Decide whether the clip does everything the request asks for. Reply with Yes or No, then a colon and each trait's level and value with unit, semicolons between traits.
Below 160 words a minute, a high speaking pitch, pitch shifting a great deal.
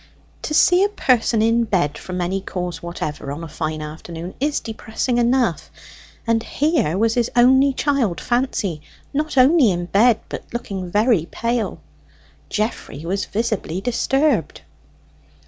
Yes: average, 140 wpm; high, 225 Hz; wide, 6.2 semitones